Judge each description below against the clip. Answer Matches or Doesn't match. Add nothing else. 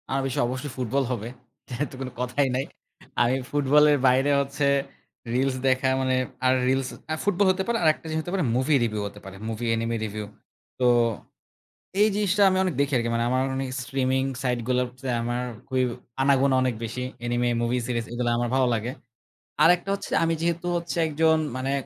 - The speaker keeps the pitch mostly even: Doesn't match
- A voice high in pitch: Doesn't match